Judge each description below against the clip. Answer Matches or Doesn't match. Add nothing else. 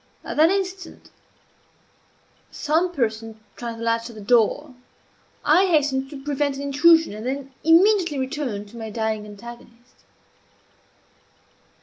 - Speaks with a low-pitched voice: Doesn't match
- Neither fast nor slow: Doesn't match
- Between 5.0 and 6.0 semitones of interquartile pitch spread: Matches